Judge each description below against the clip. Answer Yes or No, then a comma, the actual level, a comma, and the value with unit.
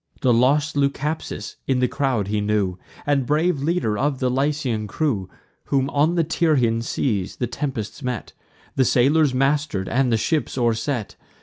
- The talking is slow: No, average, 165 wpm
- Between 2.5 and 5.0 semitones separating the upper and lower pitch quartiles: Yes, average, 4.2 semitones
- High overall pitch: No, low, 130 Hz